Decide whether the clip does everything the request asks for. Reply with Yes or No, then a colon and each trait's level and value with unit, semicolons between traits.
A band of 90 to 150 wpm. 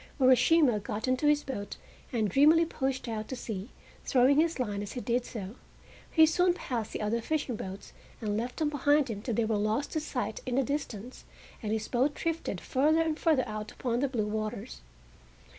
No: average, 195 wpm